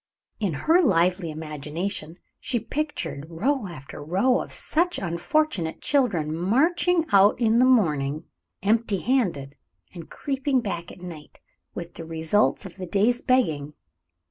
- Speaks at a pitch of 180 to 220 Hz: Yes, high, 190 Hz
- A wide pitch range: Yes, wide, 7.7 semitones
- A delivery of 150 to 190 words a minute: No, slow, 135 wpm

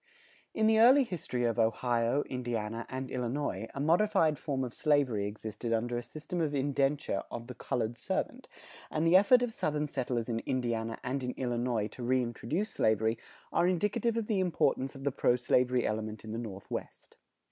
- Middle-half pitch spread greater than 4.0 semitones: Yes, average, 5.0 semitones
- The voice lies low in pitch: Yes, low, 125 Hz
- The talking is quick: No, average, 175 wpm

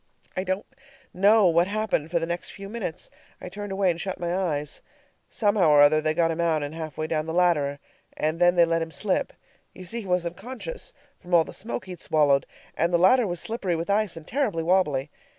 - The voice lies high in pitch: No, medium, 175 Hz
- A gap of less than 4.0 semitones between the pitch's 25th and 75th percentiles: Yes, average, 3.4 semitones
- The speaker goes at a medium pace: No, fast, 220 wpm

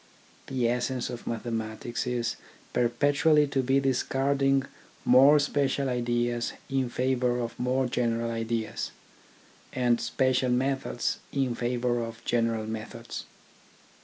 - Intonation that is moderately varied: No, narrow, 2.2 semitones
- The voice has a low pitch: Yes, low, 125 Hz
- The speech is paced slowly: Yes, slow, 115 wpm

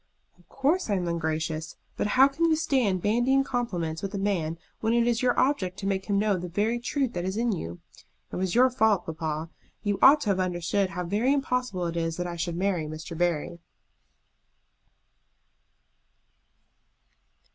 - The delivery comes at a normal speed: Yes, average, 180 wpm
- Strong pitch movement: Yes, wide, 5.9 semitones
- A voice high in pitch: Yes, high, 195 Hz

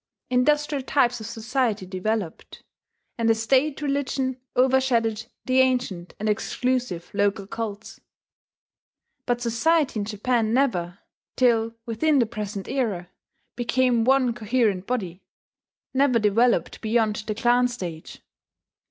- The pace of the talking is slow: Yes, slow, 115 wpm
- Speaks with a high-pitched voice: Yes, high, 235 Hz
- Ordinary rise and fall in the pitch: Yes, average, 3.3 semitones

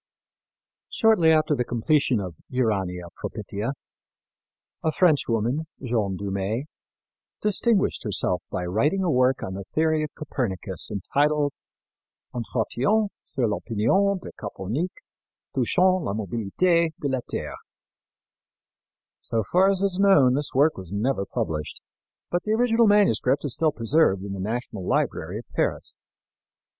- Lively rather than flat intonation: Yes, wide, 8.1 semitones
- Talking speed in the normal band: No, slow, 130 wpm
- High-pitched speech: No, low, 130 Hz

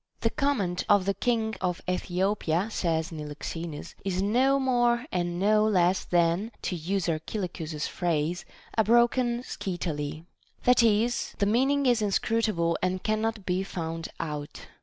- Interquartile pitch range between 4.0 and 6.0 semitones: Yes, average, 5.0 semitones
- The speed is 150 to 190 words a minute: No, average, 140 wpm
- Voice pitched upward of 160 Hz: Yes, high, 190 Hz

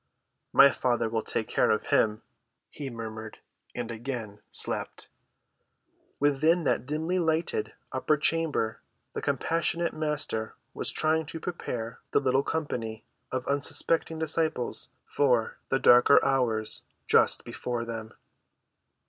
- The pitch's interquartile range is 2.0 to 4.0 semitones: No, wide, 5.5 semitones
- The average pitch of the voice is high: No, low, 135 Hz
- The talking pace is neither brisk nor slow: No, slow, 115 wpm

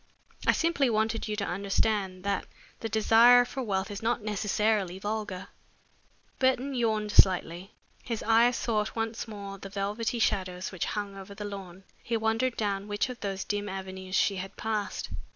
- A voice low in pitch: No, high, 210 Hz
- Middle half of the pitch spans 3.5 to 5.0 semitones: No, narrow, 2.5 semitones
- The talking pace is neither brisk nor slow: Yes, average, 165 wpm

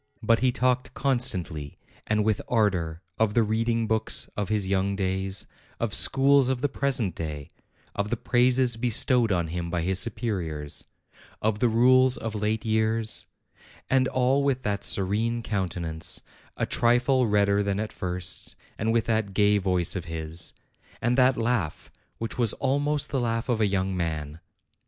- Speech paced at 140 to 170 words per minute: Yes, average, 160 wpm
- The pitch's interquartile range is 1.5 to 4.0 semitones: No, average, 4.6 semitones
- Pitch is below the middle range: Yes, low, 110 Hz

